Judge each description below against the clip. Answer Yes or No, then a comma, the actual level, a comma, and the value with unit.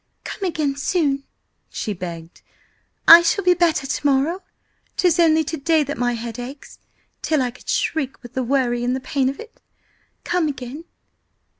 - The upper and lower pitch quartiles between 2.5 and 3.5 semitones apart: No, average, 4.6 semitones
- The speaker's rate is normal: Yes, average, 170 wpm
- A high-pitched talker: Yes, very high, 275 Hz